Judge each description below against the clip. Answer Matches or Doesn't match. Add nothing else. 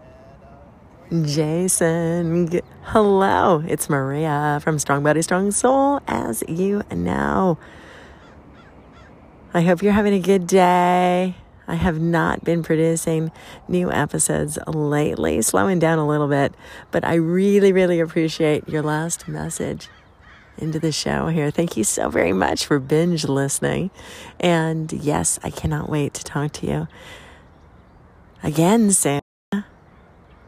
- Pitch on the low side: Doesn't match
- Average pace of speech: Doesn't match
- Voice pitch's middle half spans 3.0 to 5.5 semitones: Matches